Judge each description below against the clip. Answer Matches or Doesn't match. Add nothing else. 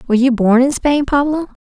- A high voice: Matches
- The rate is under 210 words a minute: Doesn't match